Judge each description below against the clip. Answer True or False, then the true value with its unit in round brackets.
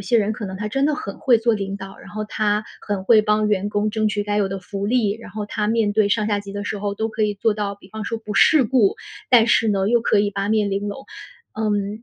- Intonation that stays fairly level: True (1.5 semitones)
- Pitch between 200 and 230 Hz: True (210 Hz)